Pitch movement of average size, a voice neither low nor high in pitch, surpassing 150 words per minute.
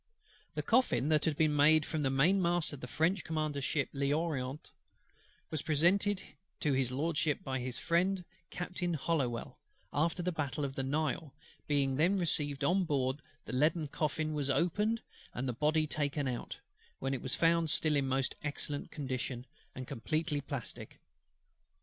Yes: average, 3.4 semitones; medium, 150 Hz; average, 160 wpm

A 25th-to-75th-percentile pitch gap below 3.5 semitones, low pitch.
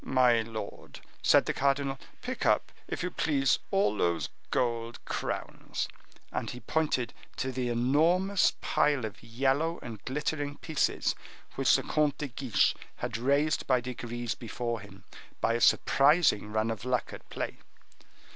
No: average, 3.8 semitones; low, 125 Hz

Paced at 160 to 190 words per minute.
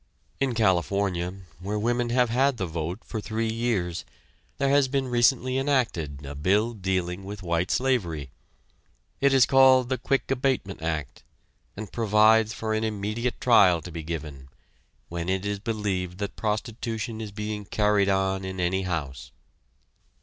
No: average, 150 wpm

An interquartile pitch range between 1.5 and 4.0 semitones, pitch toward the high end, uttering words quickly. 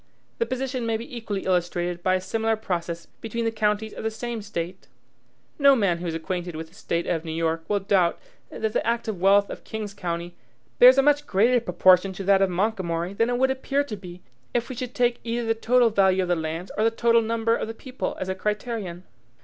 No: average, 4.5 semitones; high, 210 Hz; fast, 225 wpm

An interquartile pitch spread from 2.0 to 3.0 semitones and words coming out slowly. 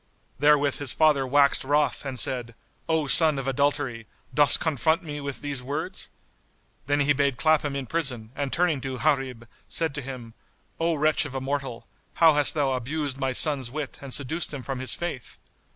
No: narrow, 2.5 semitones; average, 185 wpm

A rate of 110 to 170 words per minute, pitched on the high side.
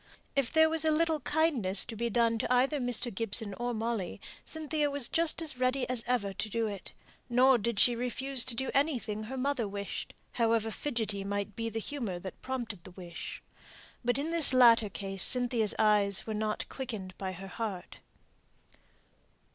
No: average, 180 wpm; high, 235 Hz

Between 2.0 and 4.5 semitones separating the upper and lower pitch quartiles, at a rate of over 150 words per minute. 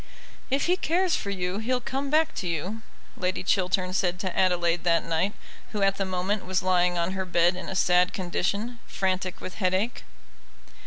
Yes: narrow, 2.4 semitones; average, 180 wpm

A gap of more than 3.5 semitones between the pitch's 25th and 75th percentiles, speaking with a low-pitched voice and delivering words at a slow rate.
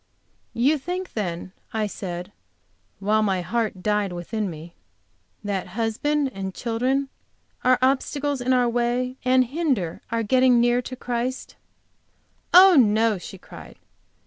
No: average, 4.2 semitones; high, 235 Hz; slow, 130 wpm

